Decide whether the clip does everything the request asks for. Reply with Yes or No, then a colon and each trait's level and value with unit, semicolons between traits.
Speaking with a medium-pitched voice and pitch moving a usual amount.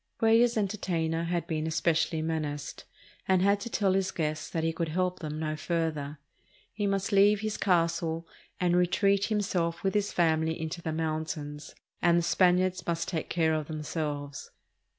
Yes: medium, 170 Hz; average, 3.1 semitones